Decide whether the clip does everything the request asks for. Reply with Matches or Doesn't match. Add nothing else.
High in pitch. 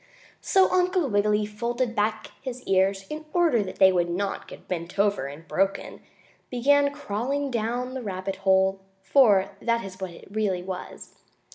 Matches